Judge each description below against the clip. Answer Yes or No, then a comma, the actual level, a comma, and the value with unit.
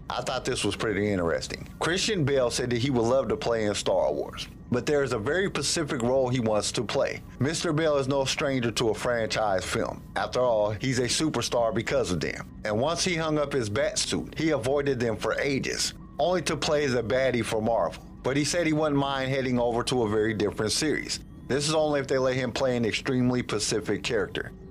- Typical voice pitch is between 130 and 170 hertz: Yes, low, 135 Hz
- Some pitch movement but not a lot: Yes, average, 3.8 semitones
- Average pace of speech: No, fast, 220 wpm